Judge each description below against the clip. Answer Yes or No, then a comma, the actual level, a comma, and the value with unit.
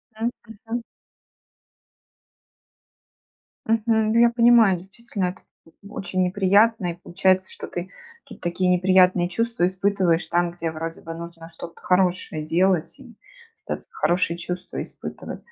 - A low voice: No, medium, 185 Hz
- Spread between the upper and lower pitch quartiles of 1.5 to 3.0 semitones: No, average, 3.9 semitones